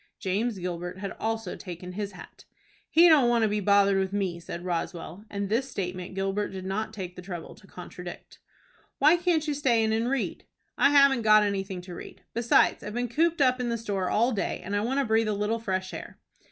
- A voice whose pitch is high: Yes, high, 205 Hz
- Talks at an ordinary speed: No, fast, 220 wpm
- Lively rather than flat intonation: No, average, 4.1 semitones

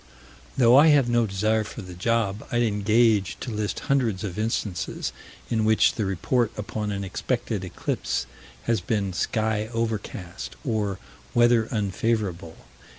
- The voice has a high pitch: No, low, 110 Hz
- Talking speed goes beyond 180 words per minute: No, average, 140 wpm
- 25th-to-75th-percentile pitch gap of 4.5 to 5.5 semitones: No, average, 2.8 semitones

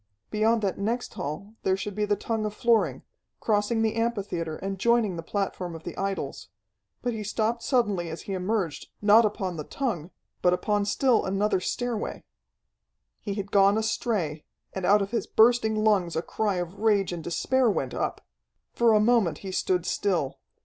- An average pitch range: Yes, average, 3.3 semitones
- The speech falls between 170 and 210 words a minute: Yes, average, 175 wpm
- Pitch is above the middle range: Yes, high, 205 Hz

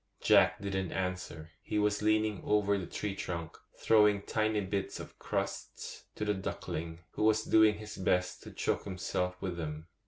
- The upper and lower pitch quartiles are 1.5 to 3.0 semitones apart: Yes, average, 2.7 semitones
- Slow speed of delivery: No, average, 165 wpm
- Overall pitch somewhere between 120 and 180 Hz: No, low, 100 Hz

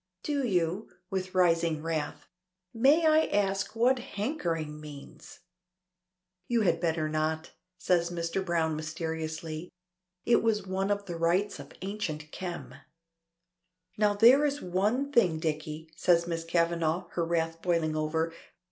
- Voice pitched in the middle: Yes, medium, 170 Hz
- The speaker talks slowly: Yes, slow, 130 wpm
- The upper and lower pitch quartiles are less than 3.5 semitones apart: No, average, 4.1 semitones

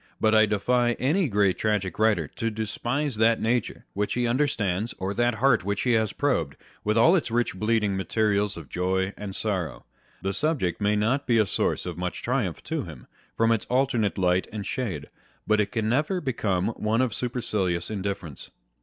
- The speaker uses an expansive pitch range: No, average, 3.7 semitones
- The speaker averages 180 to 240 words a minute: Yes, average, 185 wpm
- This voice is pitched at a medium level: No, low, 110 Hz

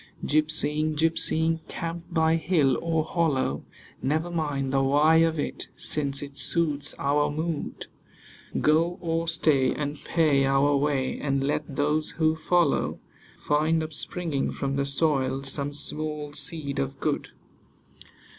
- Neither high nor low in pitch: Yes, medium, 150 Hz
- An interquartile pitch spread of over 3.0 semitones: No, narrow, 2.5 semitones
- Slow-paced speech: Yes, slow, 130 wpm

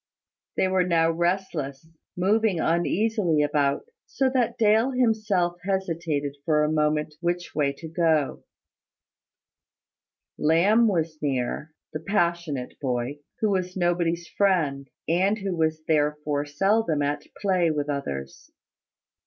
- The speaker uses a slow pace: Yes, slow, 120 wpm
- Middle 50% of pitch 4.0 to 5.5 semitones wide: Yes, average, 4.3 semitones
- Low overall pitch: No, medium, 165 Hz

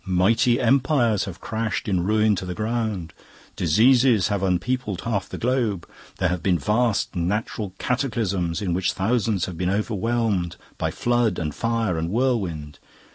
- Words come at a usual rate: Yes, average, 150 wpm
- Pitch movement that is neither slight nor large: Yes, average, 4.5 semitones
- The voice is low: Yes, low, 105 Hz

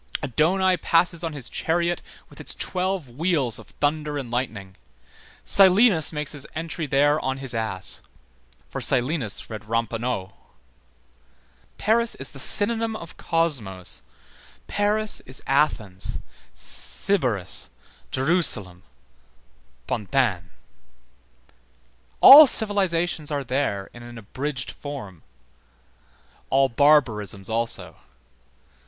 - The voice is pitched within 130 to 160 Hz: Yes, medium, 140 Hz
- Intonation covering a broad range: Yes, wide, 6.7 semitones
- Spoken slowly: Yes, slow, 100 wpm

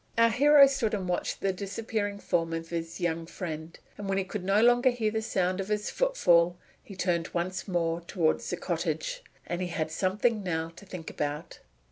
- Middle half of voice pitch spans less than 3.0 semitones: No, average, 4.1 semitones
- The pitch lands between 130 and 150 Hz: No, medium, 185 Hz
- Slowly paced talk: No, average, 195 wpm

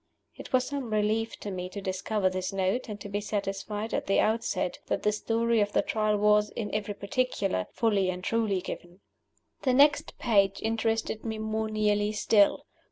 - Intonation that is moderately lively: No, narrow, 2.1 semitones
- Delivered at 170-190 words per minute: Yes, average, 180 wpm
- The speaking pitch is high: Yes, high, 210 Hz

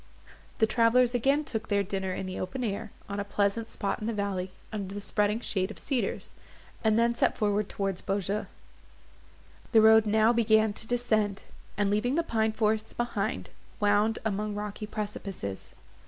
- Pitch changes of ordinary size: No, narrow, 1.8 semitones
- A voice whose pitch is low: No, high, 215 Hz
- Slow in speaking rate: No, average, 170 wpm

